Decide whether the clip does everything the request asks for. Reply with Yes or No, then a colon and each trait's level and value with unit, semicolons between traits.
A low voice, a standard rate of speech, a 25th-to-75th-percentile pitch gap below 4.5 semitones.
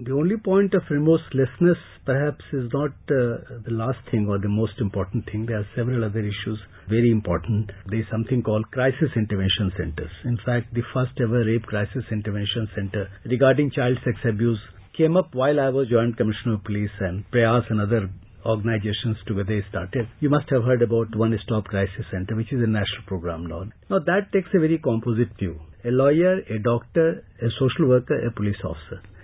Yes: low, 115 Hz; average, 190 wpm; average, 4.0 semitones